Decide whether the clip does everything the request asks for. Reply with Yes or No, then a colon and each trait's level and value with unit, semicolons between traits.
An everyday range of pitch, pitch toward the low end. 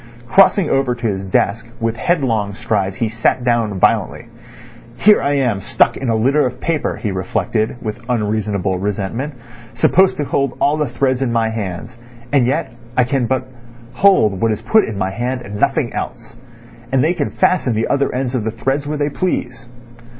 Yes: average, 4.3 semitones; low, 120 Hz